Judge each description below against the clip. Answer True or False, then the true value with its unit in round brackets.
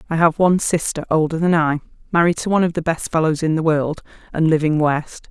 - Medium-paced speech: False (225 wpm)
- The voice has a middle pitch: True (160 Hz)